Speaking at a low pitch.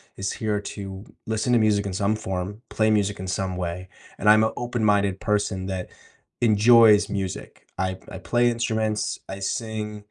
Yes: low, 105 Hz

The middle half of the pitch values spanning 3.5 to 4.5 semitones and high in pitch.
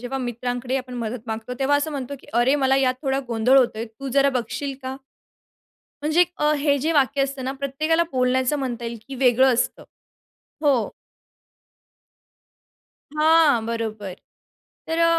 No: average, 2.7 semitones; very high, 265 Hz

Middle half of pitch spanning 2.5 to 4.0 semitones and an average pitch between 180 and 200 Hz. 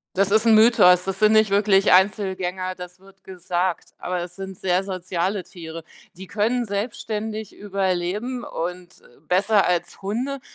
Yes: average, 2.8 semitones; high, 190 Hz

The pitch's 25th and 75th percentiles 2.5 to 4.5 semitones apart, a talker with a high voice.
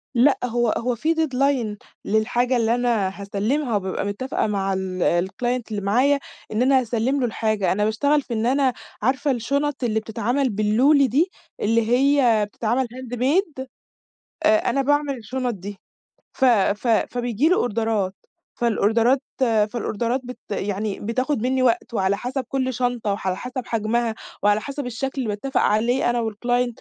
Yes: average, 3.5 semitones; high, 240 Hz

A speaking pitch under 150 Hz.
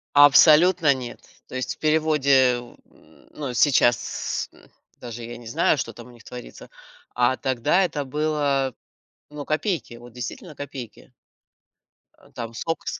Yes: low, 135 Hz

